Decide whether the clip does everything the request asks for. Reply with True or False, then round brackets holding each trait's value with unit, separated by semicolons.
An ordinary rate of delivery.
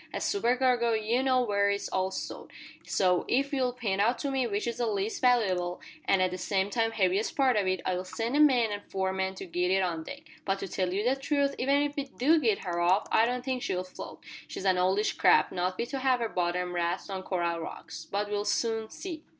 False (240 wpm)